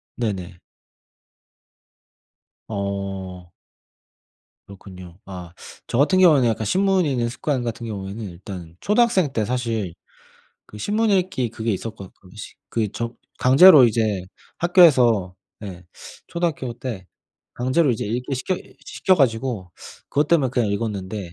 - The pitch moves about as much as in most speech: No, wide, 5.9 semitones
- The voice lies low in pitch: Yes, low, 115 Hz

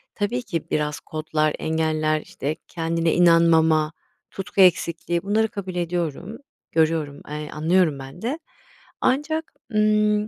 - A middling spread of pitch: Yes, average, 4.7 semitones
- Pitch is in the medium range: Yes, medium, 165 Hz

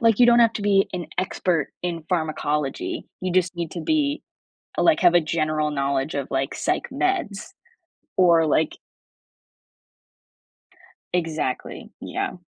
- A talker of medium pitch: Yes, medium, 175 Hz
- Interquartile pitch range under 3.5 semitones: No, average, 4.8 semitones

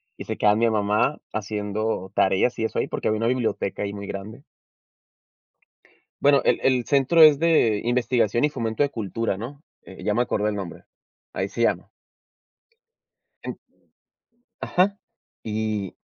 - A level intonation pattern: No, average, 3.8 semitones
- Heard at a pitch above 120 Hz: No, low, 110 Hz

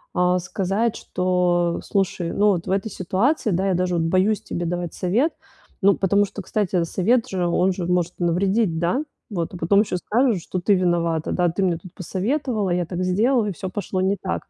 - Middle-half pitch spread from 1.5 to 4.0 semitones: Yes, narrow, 2.4 semitones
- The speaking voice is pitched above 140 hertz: Yes, medium, 185 Hz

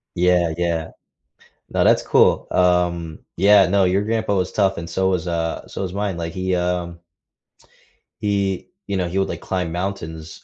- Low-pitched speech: Yes, very low, 90 Hz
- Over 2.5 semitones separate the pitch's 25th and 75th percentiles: No, narrow, 2.2 semitones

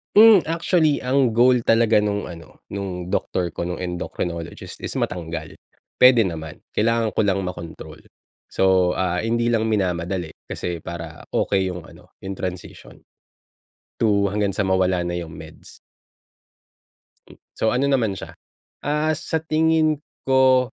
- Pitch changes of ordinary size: No, wide, 6.1 semitones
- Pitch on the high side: No, low, 100 Hz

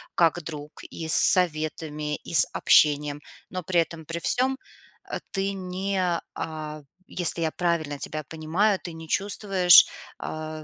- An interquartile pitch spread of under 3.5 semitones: Yes, average, 2.9 semitones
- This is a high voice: No, medium, 165 Hz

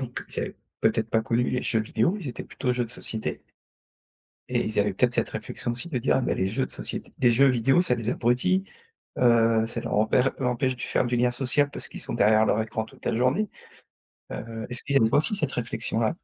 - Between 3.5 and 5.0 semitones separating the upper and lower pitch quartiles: No, narrow, 2.6 semitones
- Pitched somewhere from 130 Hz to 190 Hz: No, low, 120 Hz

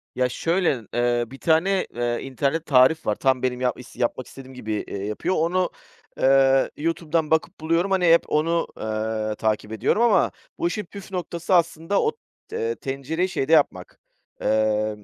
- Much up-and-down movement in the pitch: Yes, wide, 5.9 semitones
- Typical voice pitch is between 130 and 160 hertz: Yes, medium, 140 Hz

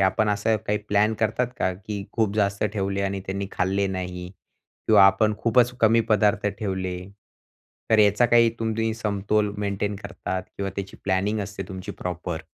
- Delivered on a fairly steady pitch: Yes, narrow, 2.0 semitones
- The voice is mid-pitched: No, low, 100 Hz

